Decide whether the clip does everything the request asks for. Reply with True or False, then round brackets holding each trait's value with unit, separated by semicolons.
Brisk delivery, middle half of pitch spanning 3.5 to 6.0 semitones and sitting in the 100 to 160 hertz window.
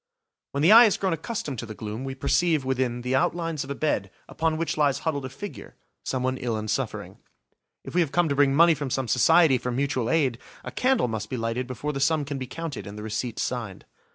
True (230 wpm; 4.7 semitones; 135 Hz)